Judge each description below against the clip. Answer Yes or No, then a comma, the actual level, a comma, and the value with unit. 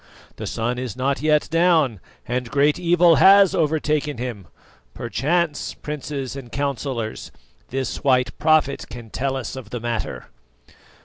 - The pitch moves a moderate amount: Yes, average, 3.8 semitones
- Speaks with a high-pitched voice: No, medium, 140 Hz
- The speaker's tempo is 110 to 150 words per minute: Yes, slow, 135 wpm